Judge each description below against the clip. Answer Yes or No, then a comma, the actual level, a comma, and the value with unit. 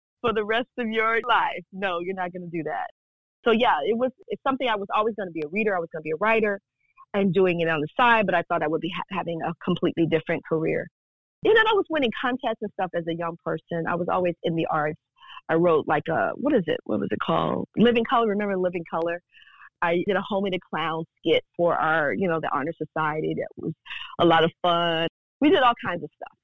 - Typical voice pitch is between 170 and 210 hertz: Yes, medium, 185 Hz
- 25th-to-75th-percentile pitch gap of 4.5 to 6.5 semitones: Yes, average, 5.2 semitones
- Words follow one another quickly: Yes, fast, 250 wpm